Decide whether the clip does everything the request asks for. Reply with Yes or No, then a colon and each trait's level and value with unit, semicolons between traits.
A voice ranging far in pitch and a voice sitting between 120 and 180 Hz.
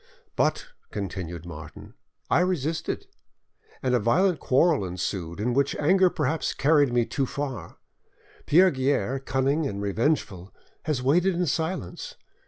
Yes: wide, 7.8 semitones; low, 135 Hz